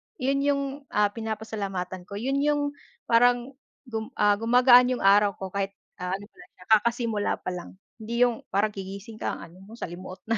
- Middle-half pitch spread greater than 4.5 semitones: No, average, 3.6 semitones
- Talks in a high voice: Yes, high, 220 Hz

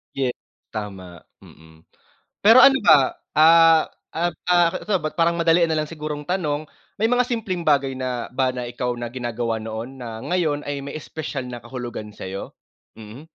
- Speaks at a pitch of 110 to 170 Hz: Yes, medium, 140 Hz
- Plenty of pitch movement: Yes, wide, 5.7 semitones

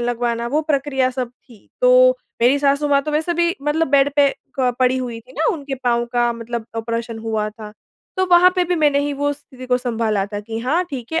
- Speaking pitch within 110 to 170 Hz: No, very high, 255 Hz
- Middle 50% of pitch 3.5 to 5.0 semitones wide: Yes, average, 3.8 semitones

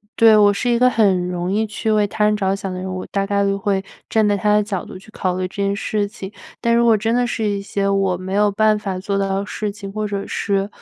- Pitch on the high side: Yes, high, 200 Hz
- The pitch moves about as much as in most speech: No, narrow, 1.6 semitones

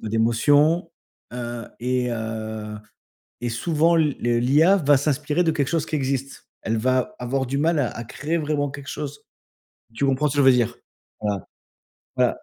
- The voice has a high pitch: No, low, 135 Hz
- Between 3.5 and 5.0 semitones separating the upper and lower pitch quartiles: Yes, average, 4.0 semitones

